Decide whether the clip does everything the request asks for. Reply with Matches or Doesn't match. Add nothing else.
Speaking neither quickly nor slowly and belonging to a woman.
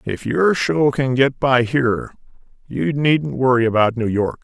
Doesn't match